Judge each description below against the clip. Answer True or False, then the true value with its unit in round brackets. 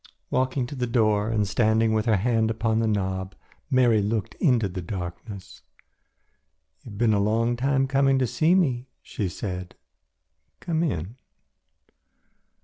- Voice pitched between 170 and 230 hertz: False (110 Hz)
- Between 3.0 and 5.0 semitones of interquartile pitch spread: True (3.7 semitones)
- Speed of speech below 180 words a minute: True (145 wpm)